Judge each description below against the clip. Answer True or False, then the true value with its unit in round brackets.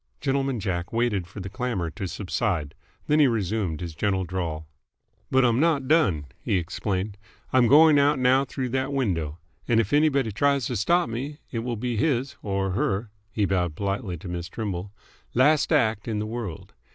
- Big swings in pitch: True (5.9 semitones)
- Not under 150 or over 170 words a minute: False (185 wpm)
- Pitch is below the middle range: True (110 Hz)